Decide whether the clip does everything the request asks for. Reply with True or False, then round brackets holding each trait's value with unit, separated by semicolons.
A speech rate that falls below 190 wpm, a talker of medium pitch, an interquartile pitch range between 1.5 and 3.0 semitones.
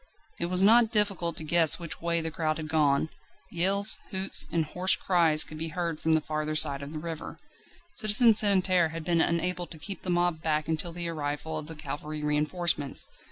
False (200 wpm; 165 Hz; 2.7 semitones)